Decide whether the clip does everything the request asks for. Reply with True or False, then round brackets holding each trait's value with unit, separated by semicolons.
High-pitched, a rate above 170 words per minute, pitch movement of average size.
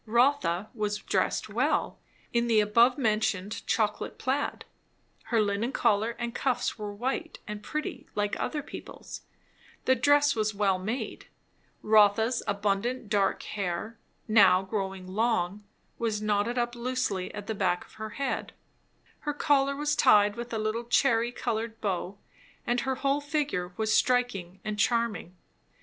False (220 Hz; 140 wpm; 3.2 semitones)